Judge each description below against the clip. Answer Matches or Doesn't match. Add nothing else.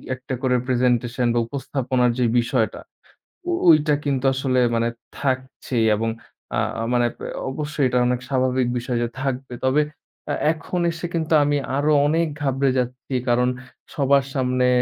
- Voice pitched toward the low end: Matches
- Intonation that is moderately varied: Doesn't match